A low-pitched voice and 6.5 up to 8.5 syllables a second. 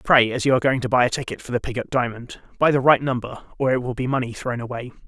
Yes: low, 125 Hz; 6.8 syllables/s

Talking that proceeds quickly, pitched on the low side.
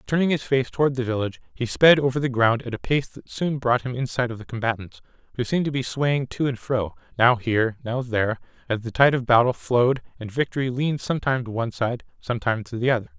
Yes: fast, 225 wpm; low, 125 Hz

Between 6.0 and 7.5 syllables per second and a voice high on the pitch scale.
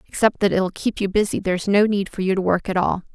Yes: 6.2 syllables/s; high, 195 Hz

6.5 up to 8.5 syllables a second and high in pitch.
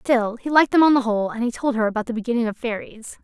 Yes: 7.0 syllables/s; high, 235 Hz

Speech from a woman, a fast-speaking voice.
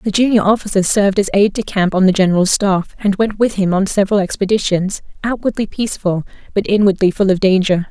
No: female; average, 195 wpm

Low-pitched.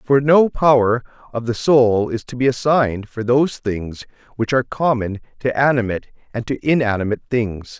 Yes: low, 120 Hz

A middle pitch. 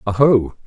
No: low, 115 Hz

